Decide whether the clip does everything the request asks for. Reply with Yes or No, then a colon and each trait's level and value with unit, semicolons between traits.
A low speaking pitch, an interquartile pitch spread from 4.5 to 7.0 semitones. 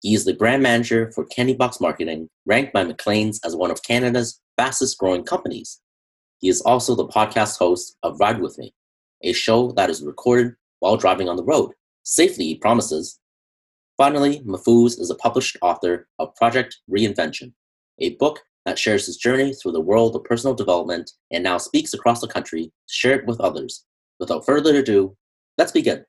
Yes: low, 115 Hz; average, 4.8 semitones